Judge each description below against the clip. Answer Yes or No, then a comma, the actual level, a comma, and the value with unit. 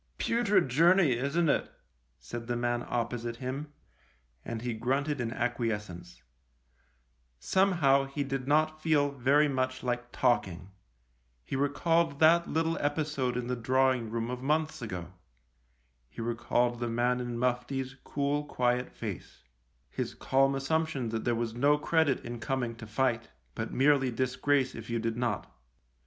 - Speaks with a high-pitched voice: No, low, 125 Hz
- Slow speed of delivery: No, average, 150 wpm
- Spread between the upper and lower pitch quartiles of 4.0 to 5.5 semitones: No, average, 3.4 semitones